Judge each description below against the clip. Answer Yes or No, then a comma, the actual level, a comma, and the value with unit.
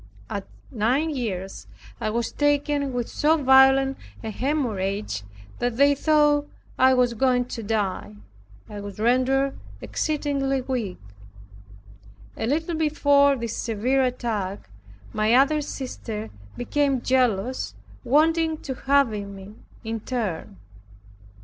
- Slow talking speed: Yes, slow, 115 wpm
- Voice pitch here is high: Yes, very high, 255 Hz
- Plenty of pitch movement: No, average, 4.4 semitones